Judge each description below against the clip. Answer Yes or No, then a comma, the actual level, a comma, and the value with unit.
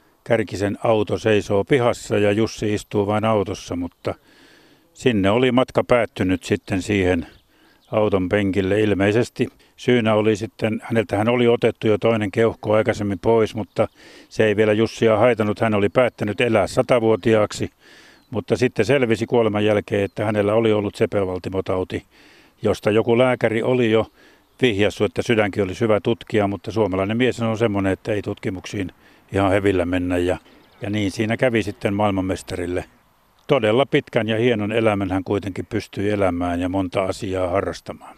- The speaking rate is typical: Yes, average, 145 wpm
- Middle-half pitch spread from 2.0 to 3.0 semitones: Yes, narrow, 2.4 semitones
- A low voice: Yes, low, 105 Hz